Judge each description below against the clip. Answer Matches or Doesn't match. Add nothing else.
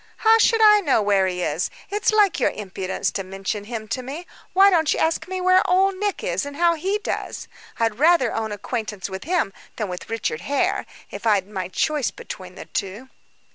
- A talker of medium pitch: Doesn't match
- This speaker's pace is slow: Doesn't match